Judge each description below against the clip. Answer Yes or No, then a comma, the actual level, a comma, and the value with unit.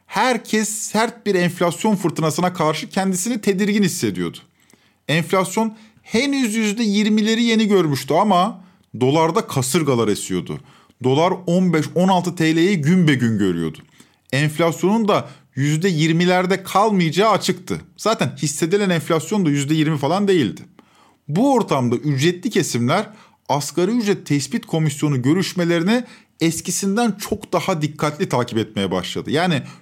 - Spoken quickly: No, average, 110 wpm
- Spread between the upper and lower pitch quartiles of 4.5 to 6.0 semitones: Yes, wide, 5.4 semitones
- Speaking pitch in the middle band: Yes, medium, 175 Hz